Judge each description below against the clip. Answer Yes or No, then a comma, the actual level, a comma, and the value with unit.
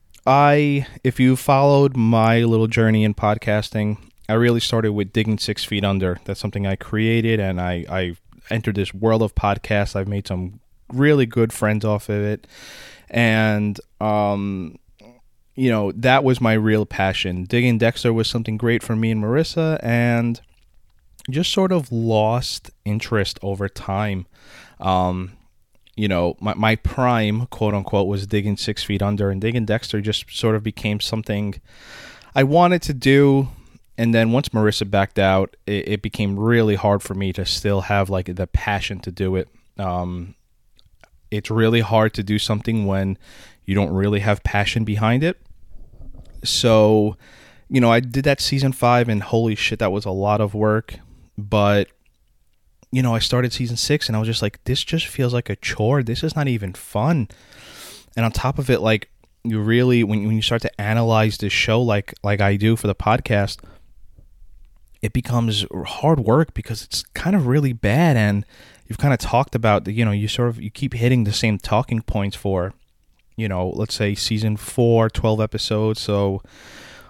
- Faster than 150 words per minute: Yes, average, 180 wpm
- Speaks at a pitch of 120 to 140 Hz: No, low, 110 Hz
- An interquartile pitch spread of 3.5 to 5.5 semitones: No, average, 2.8 semitones